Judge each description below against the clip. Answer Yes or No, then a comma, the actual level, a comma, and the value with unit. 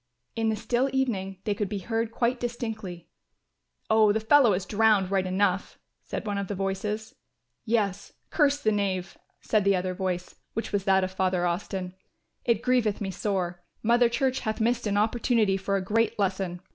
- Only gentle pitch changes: No, average, 3.0 semitones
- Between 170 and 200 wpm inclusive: Yes, average, 180 wpm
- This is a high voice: Yes, high, 205 Hz